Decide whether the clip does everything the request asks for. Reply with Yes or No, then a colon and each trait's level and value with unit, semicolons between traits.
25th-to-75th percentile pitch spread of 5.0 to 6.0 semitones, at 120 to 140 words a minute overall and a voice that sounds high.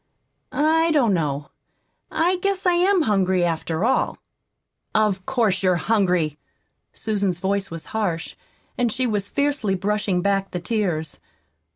Yes: wide, 5.6 semitones; slow, 135 wpm; high, 200 Hz